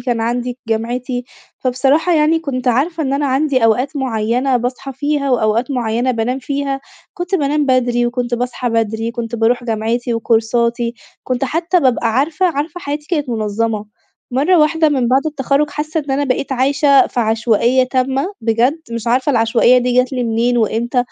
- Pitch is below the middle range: No, very high, 255 Hz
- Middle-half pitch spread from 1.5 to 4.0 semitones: Yes, average, 3.2 semitones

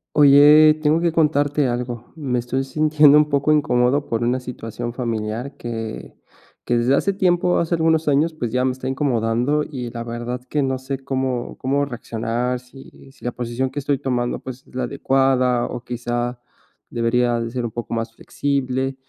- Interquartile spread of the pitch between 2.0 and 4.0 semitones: Yes, average, 3.1 semitones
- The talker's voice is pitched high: No, low, 130 Hz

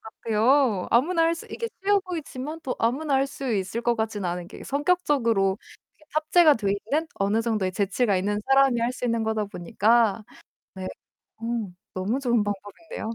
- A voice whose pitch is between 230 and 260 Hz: Yes, high, 235 Hz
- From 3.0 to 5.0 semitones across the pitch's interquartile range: No, wide, 5.6 semitones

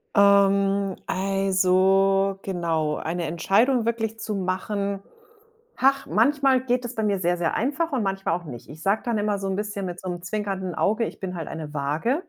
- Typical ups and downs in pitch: Yes, average, 3.3 semitones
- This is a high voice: Yes, high, 195 Hz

